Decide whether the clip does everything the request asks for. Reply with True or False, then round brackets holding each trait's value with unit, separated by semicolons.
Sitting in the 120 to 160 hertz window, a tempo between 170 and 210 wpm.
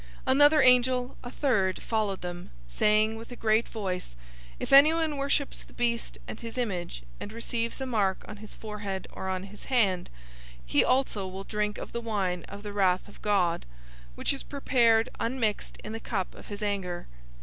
False (215 Hz; 185 wpm)